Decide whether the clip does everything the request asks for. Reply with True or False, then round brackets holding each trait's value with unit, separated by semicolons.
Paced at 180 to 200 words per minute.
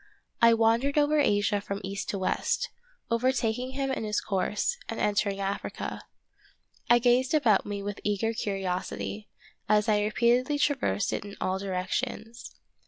False (150 wpm)